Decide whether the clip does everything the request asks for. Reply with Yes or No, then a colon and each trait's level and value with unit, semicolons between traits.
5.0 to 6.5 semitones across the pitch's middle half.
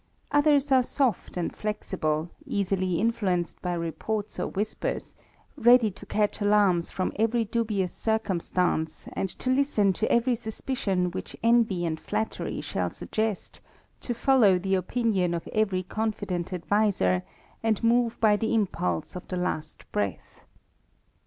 No: average, 4.1 semitones